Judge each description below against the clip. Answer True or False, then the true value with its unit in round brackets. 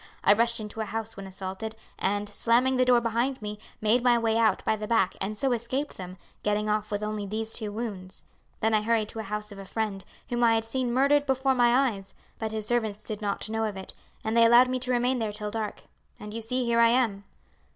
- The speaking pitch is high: True (220 Hz)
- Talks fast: True (240 wpm)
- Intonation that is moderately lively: False (2.3 semitones)